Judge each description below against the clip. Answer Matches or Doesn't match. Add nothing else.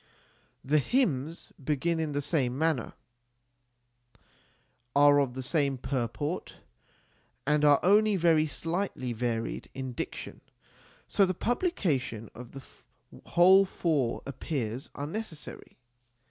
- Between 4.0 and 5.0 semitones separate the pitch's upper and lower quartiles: Matches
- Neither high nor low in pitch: Matches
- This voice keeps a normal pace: Doesn't match